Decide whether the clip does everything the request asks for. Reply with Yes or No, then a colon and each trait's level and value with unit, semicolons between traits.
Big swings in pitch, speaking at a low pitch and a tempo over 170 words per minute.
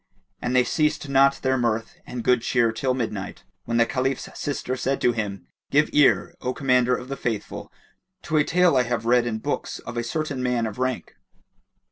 No: narrow, 2.5 semitones; low, 125 Hz; average, 195 wpm